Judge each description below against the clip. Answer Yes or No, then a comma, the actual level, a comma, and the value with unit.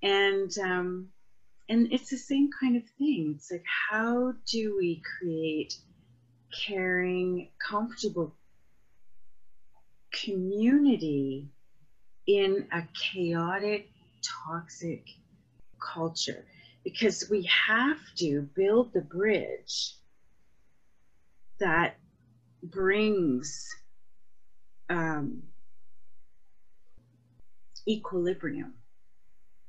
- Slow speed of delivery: Yes, slow, 70 wpm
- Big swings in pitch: Yes, wide, 8.3 semitones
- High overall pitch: No, medium, 175 Hz